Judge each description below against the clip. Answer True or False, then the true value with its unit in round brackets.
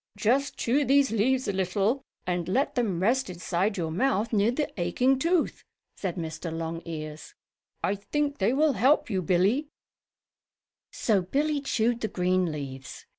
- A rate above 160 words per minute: False (150 wpm)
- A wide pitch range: True (7.0 semitones)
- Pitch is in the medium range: False (205 Hz)